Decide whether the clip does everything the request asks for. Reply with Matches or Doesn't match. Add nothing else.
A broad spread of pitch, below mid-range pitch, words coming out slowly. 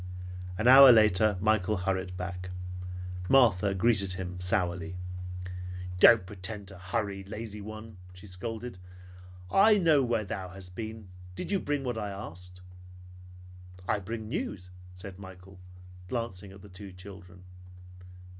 Doesn't match